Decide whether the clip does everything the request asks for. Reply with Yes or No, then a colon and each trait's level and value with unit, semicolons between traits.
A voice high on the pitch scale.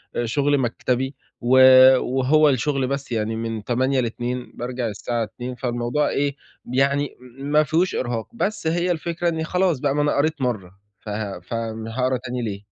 No: low, 130 Hz